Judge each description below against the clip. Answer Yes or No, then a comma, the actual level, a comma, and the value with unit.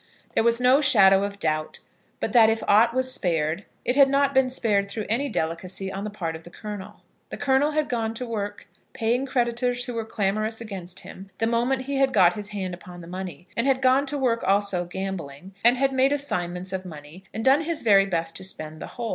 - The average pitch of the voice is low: No, high, 215 Hz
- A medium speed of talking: No, fast, 220 wpm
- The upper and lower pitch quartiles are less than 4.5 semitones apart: No, wide, 5.4 semitones